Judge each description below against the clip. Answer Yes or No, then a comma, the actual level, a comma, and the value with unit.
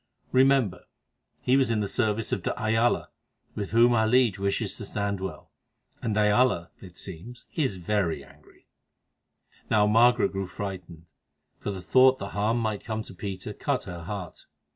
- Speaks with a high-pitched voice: No, low, 105 Hz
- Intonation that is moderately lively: Yes, average, 3.7 semitones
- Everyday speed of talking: Yes, average, 165 wpm